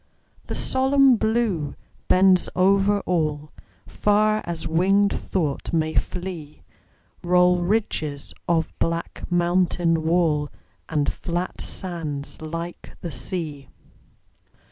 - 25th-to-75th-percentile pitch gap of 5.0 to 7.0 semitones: No, average, 3.3 semitones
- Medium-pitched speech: Yes, medium, 175 Hz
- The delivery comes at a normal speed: No, slow, 100 wpm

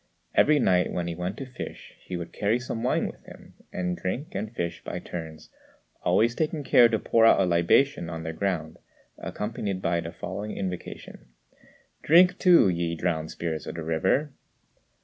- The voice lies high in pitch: No, very low, 95 Hz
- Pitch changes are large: Yes, wide, 5.7 semitones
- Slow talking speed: No, average, 175 wpm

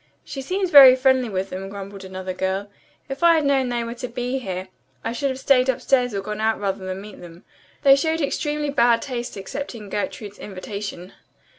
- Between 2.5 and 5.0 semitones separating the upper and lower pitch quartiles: No, wide, 5.6 semitones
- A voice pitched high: Yes, high, 235 Hz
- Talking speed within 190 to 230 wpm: Yes, average, 195 wpm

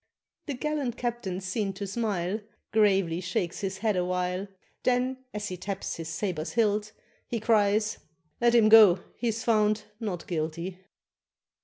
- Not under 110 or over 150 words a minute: Yes, average, 140 wpm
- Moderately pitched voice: No, high, 205 Hz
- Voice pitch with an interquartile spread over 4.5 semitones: No, average, 3.6 semitones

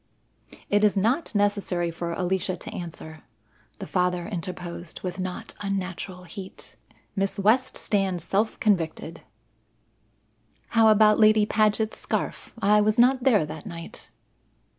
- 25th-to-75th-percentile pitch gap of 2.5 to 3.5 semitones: Yes, average, 3.1 semitones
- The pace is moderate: No, slow, 125 wpm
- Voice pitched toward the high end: Yes, high, 195 Hz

